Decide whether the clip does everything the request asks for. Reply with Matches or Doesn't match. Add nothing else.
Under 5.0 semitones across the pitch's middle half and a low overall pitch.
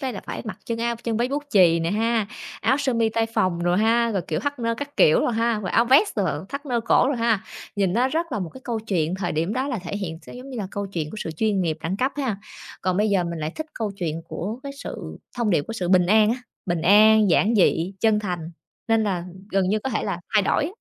Doesn't match